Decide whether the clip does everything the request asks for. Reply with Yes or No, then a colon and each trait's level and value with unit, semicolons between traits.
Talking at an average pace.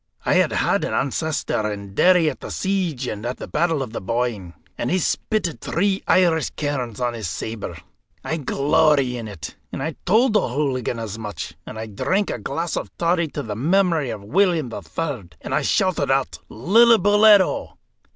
Yes: average, 180 wpm